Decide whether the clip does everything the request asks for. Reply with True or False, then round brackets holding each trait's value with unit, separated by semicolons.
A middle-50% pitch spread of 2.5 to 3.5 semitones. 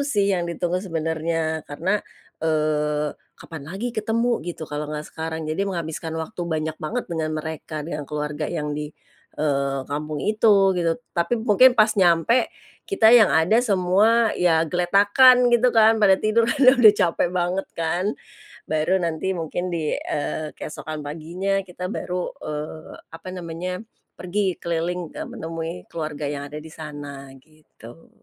False (4.1 semitones)